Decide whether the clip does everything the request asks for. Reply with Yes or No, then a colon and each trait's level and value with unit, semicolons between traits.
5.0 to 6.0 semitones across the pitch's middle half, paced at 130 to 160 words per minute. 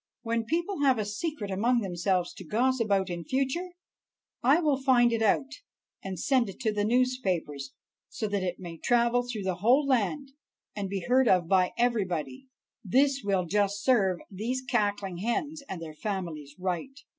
No: wide, 5.5 semitones; average, 170 wpm